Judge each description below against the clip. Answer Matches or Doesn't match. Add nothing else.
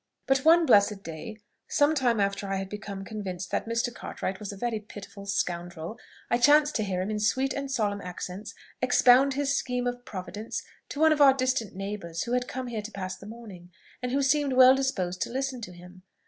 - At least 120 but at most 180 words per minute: Doesn't match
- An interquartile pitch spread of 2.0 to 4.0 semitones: Doesn't match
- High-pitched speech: Matches